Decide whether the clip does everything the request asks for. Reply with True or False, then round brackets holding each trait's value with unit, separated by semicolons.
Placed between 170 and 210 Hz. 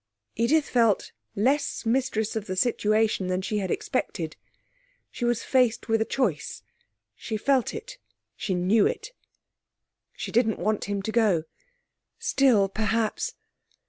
False (220 Hz)